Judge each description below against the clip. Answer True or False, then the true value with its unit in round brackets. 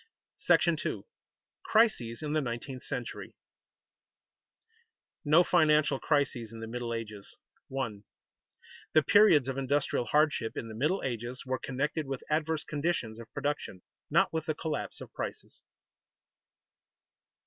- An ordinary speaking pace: False (130 wpm)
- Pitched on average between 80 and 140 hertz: True (135 Hz)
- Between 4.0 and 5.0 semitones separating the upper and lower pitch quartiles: True (4.5 semitones)